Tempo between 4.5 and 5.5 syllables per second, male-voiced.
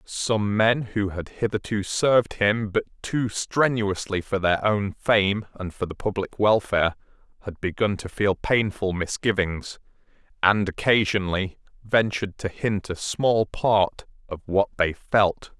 No: 4.1 syllables/s; male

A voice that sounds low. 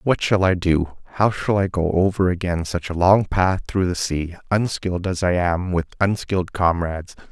Yes: very low, 90 Hz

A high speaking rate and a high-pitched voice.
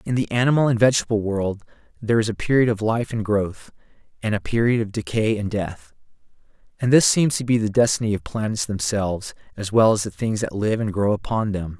No: fast, 215 wpm; low, 110 Hz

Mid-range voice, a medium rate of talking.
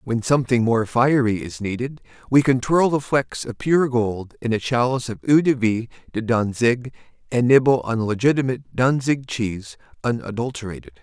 No: low, 120 Hz; average, 165 wpm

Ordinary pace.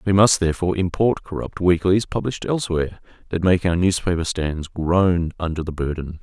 Yes: average, 165 wpm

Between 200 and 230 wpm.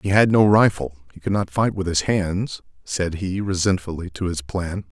Yes: fast, 205 wpm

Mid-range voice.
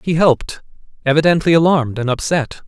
Yes: medium, 150 Hz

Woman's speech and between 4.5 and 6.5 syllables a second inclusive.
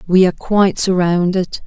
Yes: female; 5.4 syllables/s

